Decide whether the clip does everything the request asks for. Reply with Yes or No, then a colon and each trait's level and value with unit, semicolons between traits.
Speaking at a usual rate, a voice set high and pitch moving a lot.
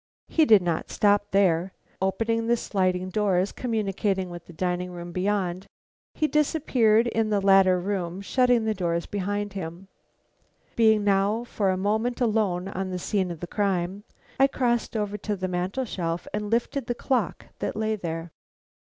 No: average, 160 wpm; high, 200 Hz; average, 3.3 semitones